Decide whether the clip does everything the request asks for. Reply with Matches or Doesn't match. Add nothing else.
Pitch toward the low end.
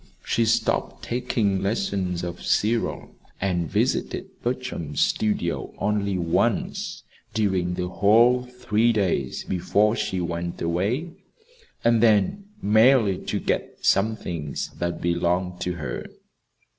Matches